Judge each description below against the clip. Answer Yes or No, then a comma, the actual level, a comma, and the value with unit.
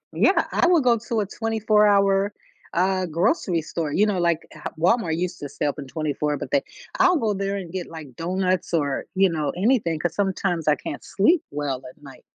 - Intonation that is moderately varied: Yes, average, 4.6 semitones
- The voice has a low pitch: No, medium, 185 Hz